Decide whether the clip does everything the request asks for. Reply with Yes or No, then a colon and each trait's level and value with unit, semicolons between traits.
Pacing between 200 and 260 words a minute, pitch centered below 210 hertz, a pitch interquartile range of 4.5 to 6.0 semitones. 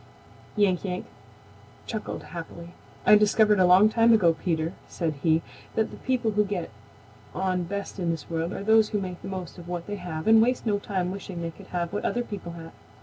No: fast, 205 wpm; medium, 185 Hz; average, 3.6 semitones